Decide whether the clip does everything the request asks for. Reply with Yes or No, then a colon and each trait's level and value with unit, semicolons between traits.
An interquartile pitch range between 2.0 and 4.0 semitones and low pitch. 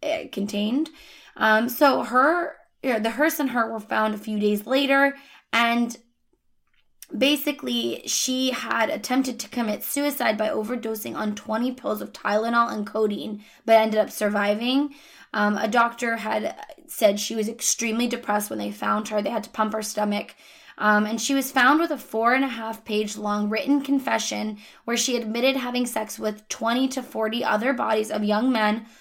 No: average, 3.6 semitones; high, 230 Hz